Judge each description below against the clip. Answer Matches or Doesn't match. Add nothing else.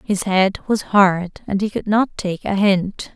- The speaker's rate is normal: Doesn't match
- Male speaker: Doesn't match